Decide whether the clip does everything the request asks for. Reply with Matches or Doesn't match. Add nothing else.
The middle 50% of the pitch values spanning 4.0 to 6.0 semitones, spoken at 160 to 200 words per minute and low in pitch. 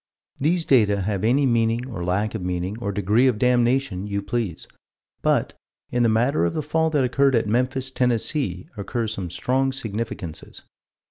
Matches